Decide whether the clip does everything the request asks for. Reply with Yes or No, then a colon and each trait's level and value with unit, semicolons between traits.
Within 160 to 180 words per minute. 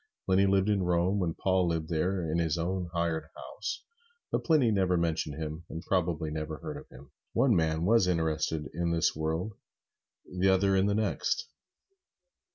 Yes: average, 170 wpm